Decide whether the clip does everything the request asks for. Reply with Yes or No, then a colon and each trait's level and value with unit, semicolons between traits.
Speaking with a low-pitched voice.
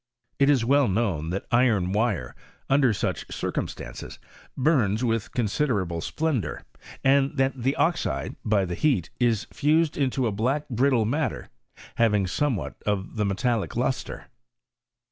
Yes: low, 120 Hz